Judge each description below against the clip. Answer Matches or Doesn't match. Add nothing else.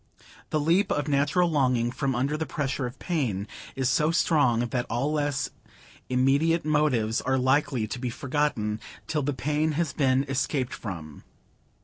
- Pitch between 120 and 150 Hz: Matches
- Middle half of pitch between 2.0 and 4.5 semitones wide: Matches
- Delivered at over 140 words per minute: Matches